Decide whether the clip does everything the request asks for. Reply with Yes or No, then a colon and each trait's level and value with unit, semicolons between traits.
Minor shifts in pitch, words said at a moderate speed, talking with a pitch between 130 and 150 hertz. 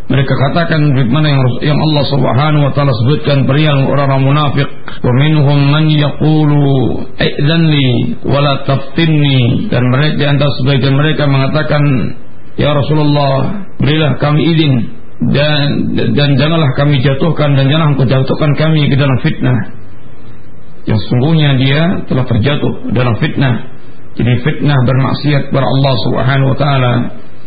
Yes: narrow, 2.2 semitones; average, 130 wpm; medium, 140 Hz